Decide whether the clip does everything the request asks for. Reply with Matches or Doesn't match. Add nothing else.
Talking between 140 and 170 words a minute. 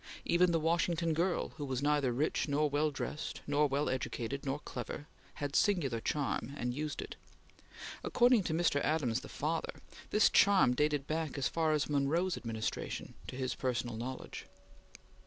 Matches